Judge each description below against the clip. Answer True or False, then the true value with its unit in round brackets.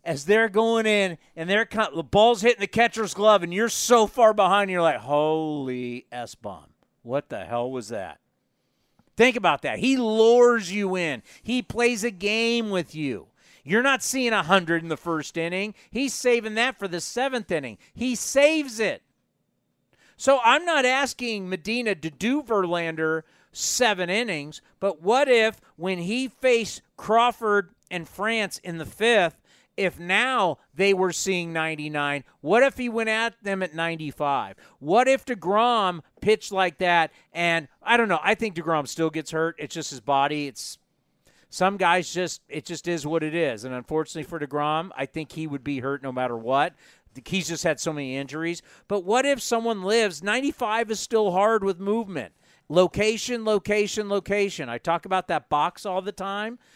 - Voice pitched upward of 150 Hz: True (190 Hz)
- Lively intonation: True (6.0 semitones)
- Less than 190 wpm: True (175 wpm)